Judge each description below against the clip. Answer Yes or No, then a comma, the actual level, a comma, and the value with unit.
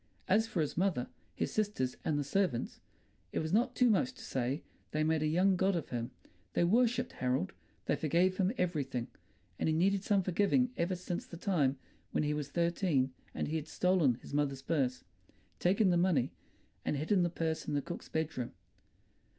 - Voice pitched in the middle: Yes, medium, 170 Hz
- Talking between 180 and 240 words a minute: Yes, average, 190 wpm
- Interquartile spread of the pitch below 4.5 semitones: No, average, 4.9 semitones